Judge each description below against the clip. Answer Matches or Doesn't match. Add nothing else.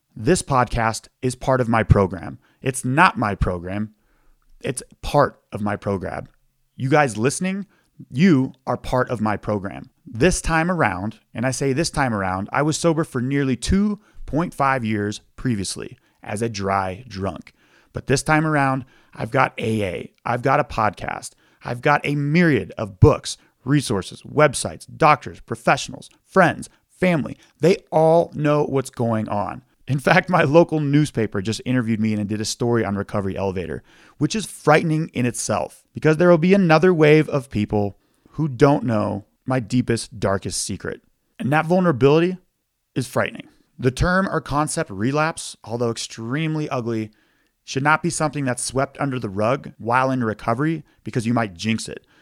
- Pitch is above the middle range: Doesn't match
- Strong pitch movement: Matches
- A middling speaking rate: Matches